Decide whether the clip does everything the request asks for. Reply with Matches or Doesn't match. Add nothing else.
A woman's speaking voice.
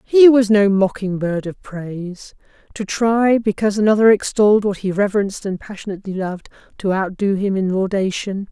Matches